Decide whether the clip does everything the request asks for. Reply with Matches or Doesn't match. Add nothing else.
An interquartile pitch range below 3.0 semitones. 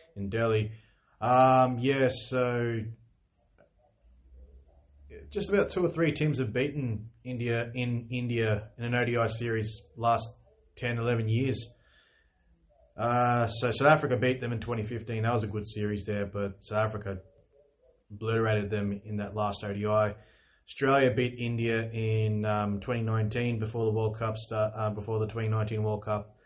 Matches